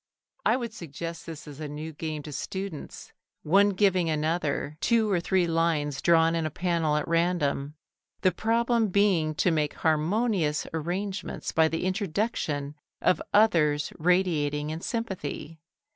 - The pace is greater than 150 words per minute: No, average, 145 wpm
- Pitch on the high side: No, medium, 165 Hz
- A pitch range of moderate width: Yes, average, 3.9 semitones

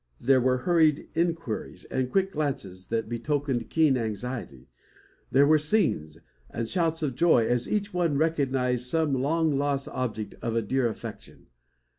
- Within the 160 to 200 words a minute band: No, average, 150 wpm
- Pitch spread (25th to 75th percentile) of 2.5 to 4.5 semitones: No, average, 5.1 semitones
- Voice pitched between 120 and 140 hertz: Yes, low, 135 Hz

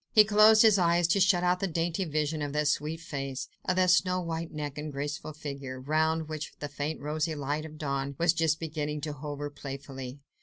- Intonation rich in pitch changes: No, narrow, 2.6 semitones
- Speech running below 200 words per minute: No, fast, 205 wpm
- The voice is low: No, medium, 155 Hz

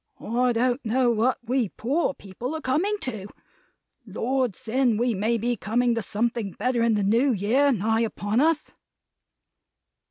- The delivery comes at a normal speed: Yes, average, 155 wpm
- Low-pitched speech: No, high, 235 Hz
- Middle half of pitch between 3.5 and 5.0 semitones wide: No, average, 2.8 semitones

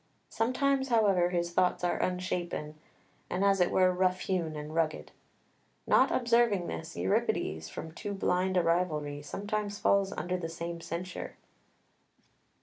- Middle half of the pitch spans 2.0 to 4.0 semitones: Yes, average, 2.9 semitones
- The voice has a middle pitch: Yes, medium, 180 Hz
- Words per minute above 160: No, average, 140 wpm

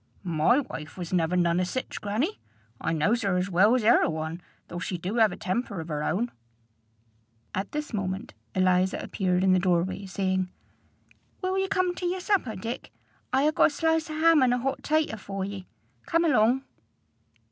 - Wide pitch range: Yes, wide, 6.8 semitones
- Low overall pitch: No, high, 200 Hz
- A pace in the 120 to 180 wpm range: No, average, 195 wpm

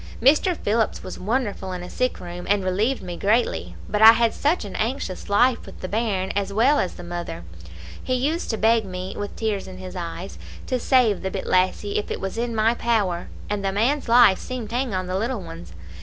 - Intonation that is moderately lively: Yes, average, 4.2 semitones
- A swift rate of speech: Yes, fast, 220 wpm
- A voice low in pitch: No, high, 205 Hz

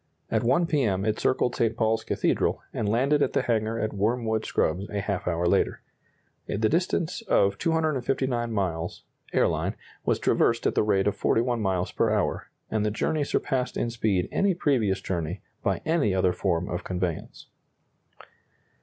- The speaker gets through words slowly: No, average, 165 wpm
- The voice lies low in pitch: Yes, low, 110 Hz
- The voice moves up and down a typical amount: Yes, average, 4.9 semitones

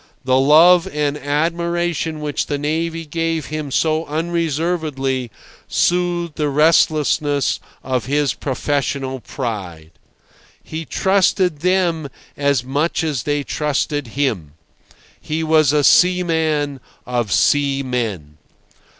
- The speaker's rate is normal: No, slow, 105 wpm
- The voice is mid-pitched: Yes, medium, 150 Hz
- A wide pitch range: No, average, 3.4 semitones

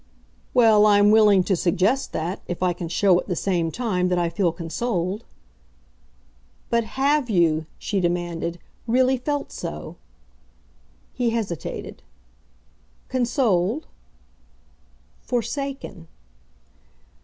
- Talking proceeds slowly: Yes, slow, 105 wpm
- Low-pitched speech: No, high, 200 Hz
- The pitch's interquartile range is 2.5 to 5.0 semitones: No, wide, 5.5 semitones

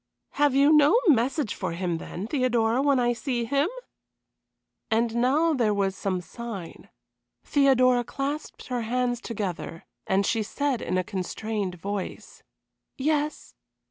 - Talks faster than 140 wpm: No, slow, 135 wpm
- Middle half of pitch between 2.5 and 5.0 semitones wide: No, wide, 5.4 semitones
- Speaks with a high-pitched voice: Yes, high, 240 Hz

